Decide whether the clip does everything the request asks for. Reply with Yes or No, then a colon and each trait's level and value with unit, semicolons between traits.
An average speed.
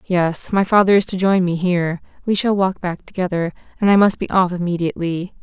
No: fast, 210 wpm